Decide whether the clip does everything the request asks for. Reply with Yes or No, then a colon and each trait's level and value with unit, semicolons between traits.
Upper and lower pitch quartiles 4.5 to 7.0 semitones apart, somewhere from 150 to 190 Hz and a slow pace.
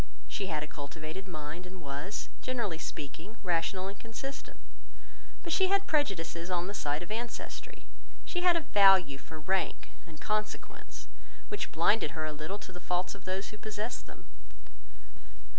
No: average, 5.0 semitones; medium, 185 Hz; average, 160 wpm